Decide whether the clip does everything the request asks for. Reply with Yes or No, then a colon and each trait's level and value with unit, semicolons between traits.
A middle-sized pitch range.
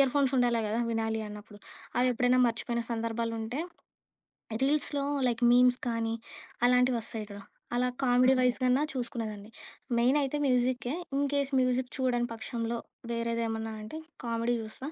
No: narrow, 2.0 semitones